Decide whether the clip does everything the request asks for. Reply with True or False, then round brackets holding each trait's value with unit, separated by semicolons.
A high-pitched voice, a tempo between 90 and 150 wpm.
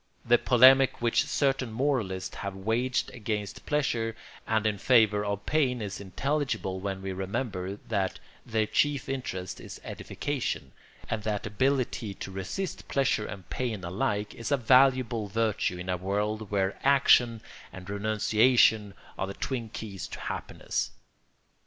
False (110 Hz; 140 wpm)